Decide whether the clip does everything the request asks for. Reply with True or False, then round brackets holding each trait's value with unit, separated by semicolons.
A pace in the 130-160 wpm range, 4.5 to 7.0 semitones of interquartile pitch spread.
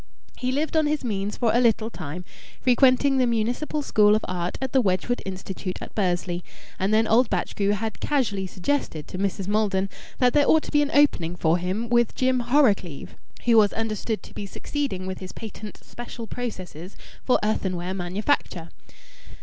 False (175 wpm; 5.0 semitones)